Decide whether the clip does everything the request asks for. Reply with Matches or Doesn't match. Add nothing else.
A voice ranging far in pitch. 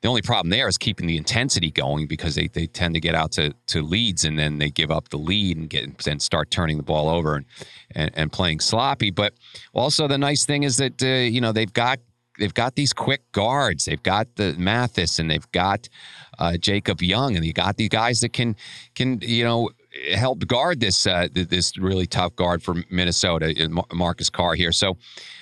Matches